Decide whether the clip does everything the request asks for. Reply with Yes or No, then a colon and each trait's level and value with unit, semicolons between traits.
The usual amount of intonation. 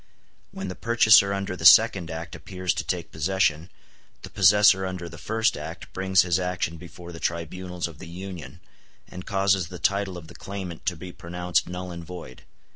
No: narrow, 2.2 semitones